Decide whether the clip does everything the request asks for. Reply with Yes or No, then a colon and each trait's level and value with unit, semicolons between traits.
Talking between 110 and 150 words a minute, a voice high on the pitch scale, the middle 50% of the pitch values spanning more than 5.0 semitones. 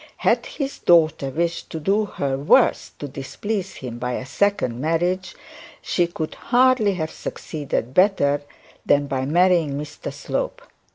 No: average, 145 wpm; medium, 160 Hz; wide, 5.5 semitones